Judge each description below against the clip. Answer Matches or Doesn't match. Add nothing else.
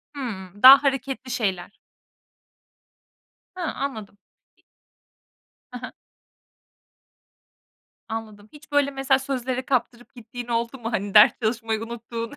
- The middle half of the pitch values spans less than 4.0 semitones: Matches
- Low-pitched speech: Doesn't match